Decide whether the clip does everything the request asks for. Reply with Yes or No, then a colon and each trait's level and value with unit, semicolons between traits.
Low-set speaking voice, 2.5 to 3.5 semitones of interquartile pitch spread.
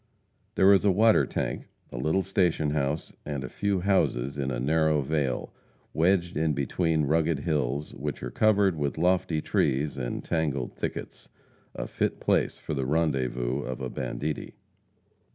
No: very low, 75 Hz; average, 4.1 semitones